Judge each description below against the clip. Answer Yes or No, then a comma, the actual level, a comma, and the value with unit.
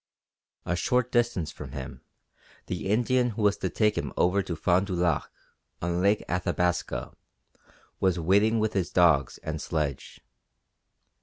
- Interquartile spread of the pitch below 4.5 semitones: Yes, average, 3.8 semitones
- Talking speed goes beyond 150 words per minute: No, average, 145 wpm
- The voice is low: Yes, very low, 90 Hz